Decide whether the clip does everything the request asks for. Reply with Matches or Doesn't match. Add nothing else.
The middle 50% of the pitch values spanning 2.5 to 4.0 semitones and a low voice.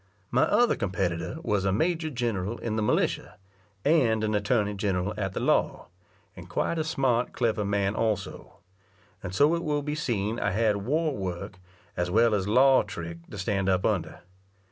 Doesn't match